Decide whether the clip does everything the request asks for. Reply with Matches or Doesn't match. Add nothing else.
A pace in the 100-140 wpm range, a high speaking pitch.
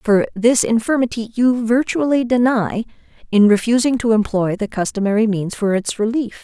Doesn't match